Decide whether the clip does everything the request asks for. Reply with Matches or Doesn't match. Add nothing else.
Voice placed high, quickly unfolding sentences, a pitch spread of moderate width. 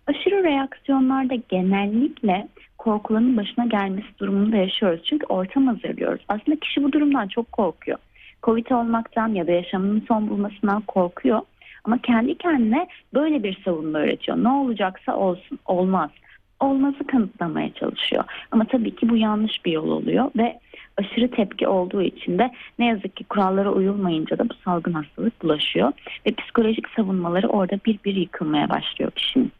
Matches